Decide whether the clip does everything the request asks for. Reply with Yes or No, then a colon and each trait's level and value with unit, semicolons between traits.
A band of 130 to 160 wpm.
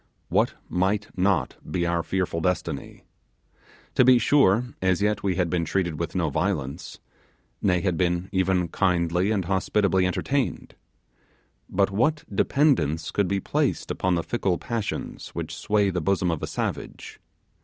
Yes: average, 150 wpm